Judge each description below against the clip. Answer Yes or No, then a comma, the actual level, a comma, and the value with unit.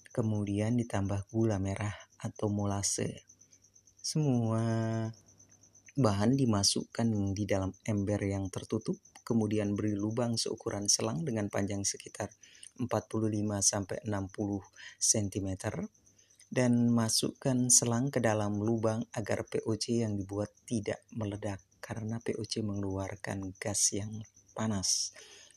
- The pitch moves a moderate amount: No, narrow, 2.1 semitones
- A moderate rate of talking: Yes, average, 100 wpm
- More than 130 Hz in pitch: No, low, 105 Hz